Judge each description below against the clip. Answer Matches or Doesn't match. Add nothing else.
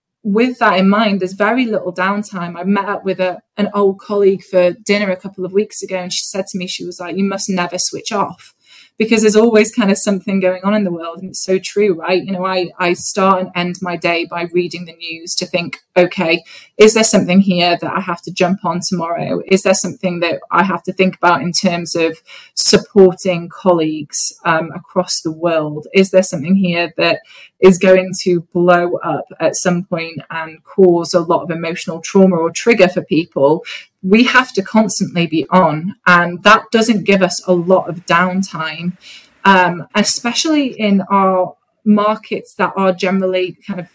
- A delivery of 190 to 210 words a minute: Matches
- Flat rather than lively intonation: Matches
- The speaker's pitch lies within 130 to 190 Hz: Matches